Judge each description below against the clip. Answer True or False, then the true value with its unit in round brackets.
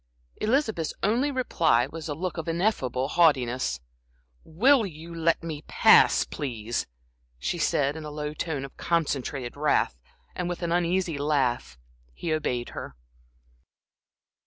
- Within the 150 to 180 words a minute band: False (135 wpm)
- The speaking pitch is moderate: True (155 Hz)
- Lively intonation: False (4.2 semitones)